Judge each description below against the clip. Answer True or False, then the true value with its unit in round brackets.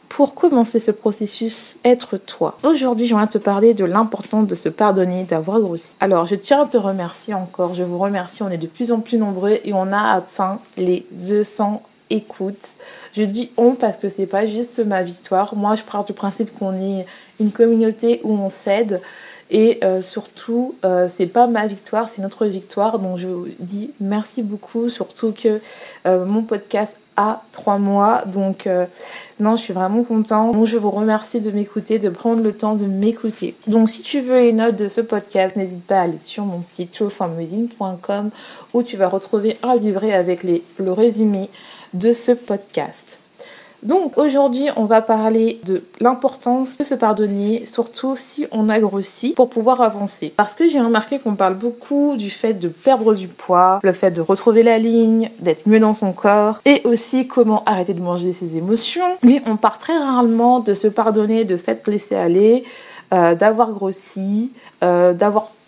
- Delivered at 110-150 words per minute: False (185 wpm)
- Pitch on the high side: True (215 Hz)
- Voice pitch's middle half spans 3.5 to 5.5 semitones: False (3.1 semitones)